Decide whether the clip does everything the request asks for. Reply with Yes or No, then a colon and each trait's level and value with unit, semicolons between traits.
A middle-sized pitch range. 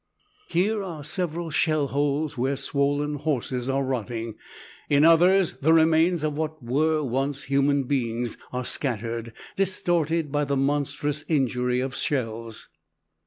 Yes: average, 3.5 semitones